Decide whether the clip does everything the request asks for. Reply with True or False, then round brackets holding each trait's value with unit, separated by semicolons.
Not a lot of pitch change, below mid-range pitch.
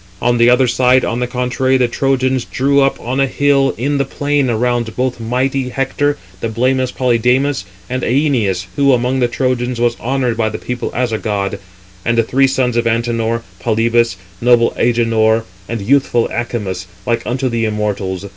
True (2.2 semitones; 120 Hz)